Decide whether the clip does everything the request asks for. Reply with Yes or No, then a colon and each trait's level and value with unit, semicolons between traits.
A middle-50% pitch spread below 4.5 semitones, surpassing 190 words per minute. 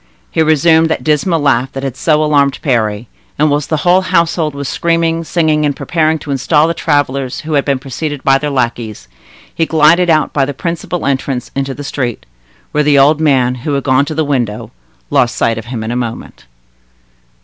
Yes: average, 3.2 semitones; average, 200 wpm